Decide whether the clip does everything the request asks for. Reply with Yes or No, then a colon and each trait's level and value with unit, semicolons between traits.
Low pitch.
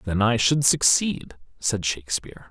Yes: low, 115 Hz